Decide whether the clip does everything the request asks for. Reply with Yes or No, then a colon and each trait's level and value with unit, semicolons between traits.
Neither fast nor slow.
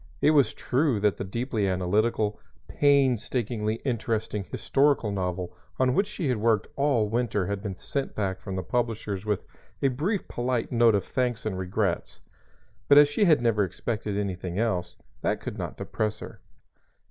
Yes: average, 165 wpm